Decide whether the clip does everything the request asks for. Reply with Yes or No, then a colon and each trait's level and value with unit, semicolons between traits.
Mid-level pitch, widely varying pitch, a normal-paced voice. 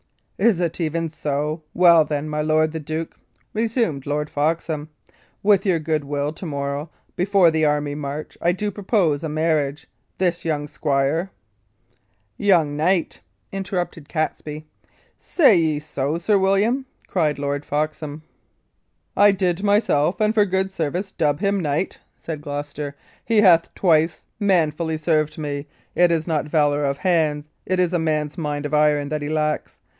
No: medium, 155 Hz; average, 3.4 semitones; average, 155 wpm